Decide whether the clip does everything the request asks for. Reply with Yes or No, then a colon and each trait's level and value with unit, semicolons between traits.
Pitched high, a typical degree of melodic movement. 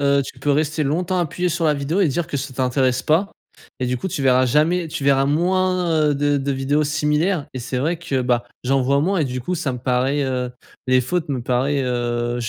No: medium, 140 Hz; average, 3.7 semitones